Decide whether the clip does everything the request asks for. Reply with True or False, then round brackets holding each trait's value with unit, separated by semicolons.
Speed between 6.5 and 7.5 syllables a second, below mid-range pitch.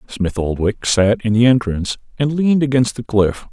False (5.0 syllables/s; 120 Hz)